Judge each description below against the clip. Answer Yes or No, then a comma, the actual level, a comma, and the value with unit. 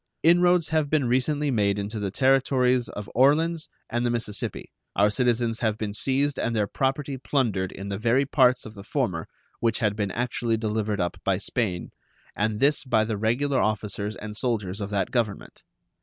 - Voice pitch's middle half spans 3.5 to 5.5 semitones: Yes, average, 4.3 semitones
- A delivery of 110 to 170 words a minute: No, average, 180 wpm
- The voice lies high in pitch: No, low, 115 Hz